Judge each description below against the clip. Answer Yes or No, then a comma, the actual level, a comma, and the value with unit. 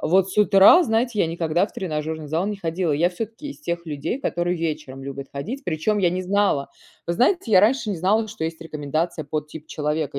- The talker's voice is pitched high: No, medium, 170 Hz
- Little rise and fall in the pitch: No, average, 4.9 semitones